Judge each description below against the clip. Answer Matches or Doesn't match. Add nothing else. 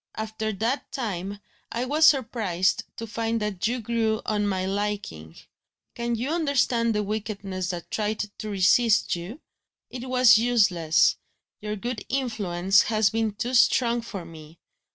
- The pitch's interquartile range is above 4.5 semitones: Doesn't match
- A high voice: Matches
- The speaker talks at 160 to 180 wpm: Doesn't match